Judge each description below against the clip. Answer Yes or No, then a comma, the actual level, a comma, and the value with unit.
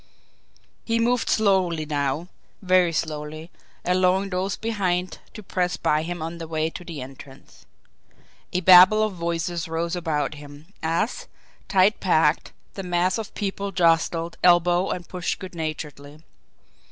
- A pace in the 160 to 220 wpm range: No, average, 140 wpm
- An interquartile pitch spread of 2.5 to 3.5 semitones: Yes, average, 2.8 semitones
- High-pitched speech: No, medium, 175 Hz